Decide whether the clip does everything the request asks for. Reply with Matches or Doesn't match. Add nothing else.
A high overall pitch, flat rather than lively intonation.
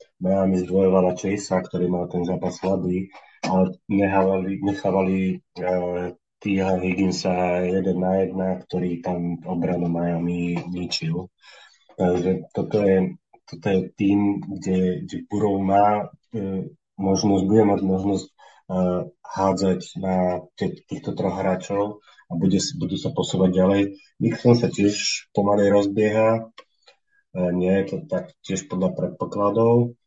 Doesn't match